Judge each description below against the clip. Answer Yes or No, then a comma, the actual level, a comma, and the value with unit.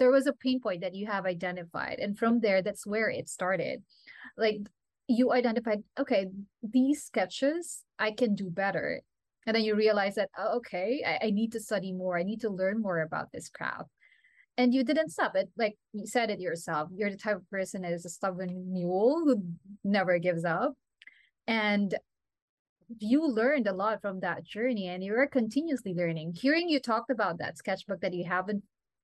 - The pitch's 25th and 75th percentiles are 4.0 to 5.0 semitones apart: Yes, average, 4.7 semitones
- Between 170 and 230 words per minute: Yes, average, 190 wpm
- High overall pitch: Yes, high, 210 Hz